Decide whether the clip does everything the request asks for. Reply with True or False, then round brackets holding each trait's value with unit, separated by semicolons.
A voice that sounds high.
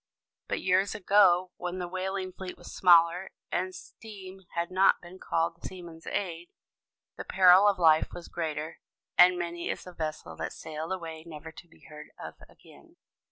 False (175 Hz)